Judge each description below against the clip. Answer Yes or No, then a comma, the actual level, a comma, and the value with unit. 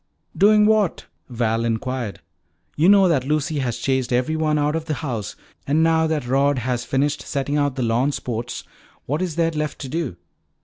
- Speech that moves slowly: No, average, 180 wpm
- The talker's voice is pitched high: No, medium, 145 Hz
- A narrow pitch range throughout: No, average, 4.1 semitones